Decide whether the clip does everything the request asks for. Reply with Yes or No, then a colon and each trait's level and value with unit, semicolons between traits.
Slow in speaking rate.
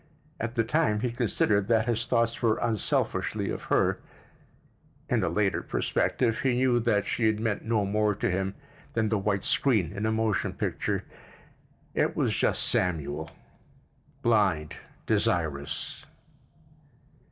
Yes: slow, 130 wpm